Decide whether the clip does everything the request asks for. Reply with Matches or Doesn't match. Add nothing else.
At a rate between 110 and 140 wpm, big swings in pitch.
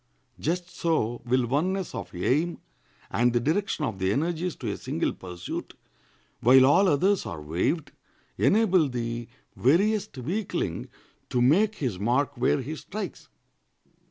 Matches